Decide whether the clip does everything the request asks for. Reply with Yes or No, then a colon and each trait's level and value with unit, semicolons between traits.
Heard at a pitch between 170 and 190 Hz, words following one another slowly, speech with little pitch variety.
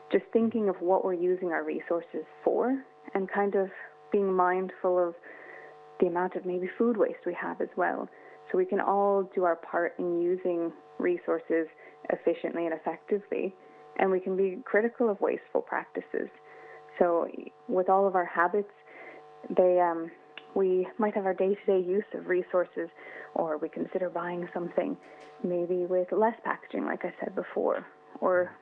No: medium, 185 Hz; average, 160 wpm; narrow, 2.0 semitones